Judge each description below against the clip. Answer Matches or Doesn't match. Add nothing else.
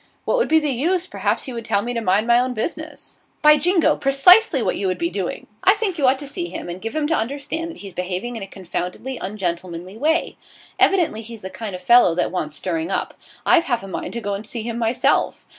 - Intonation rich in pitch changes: Matches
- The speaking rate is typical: Doesn't match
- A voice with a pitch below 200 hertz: Doesn't match